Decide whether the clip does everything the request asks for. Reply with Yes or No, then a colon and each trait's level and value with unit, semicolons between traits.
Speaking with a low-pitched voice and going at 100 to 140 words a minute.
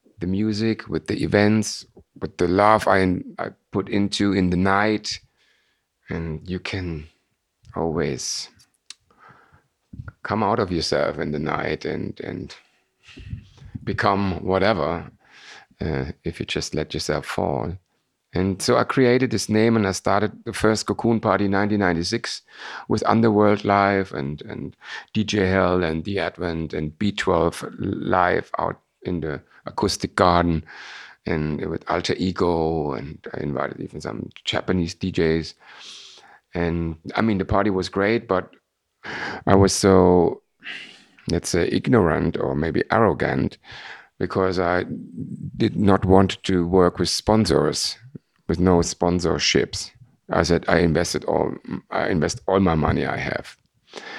Yes: very low, 95 Hz; slow, 135 wpm